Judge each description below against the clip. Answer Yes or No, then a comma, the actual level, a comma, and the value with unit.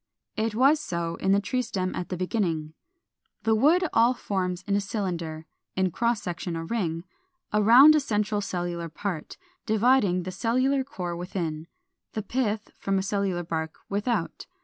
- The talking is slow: No, average, 160 wpm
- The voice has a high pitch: Yes, high, 200 Hz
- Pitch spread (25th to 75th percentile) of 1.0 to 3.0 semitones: No, average, 4.6 semitones